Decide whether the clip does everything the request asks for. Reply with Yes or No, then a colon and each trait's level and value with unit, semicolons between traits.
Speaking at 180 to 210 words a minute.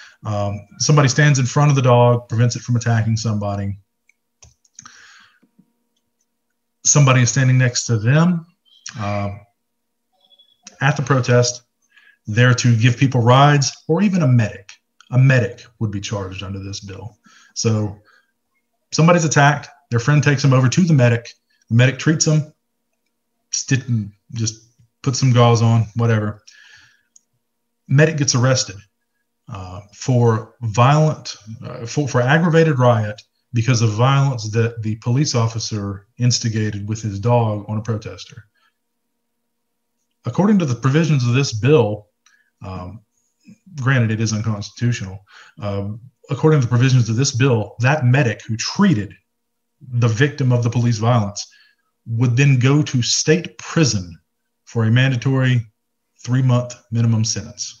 No: slow, 135 wpm